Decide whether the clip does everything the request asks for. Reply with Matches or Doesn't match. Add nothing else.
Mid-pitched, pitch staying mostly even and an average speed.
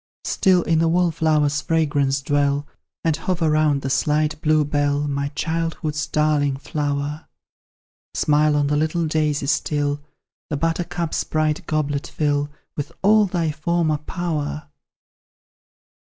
Doesn't match